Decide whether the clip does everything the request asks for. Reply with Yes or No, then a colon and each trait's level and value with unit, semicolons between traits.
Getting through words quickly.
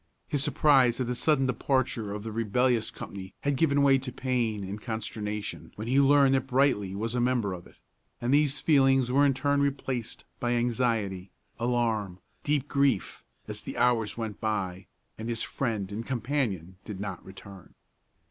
No: average, 170 wpm